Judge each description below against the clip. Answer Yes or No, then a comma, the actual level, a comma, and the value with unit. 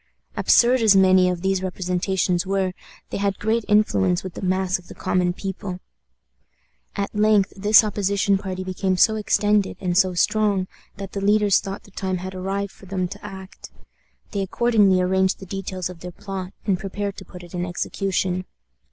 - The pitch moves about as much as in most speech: No, narrow, 1.6 semitones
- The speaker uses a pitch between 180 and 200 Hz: Yes, high, 190 Hz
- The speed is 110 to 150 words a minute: No, average, 180 wpm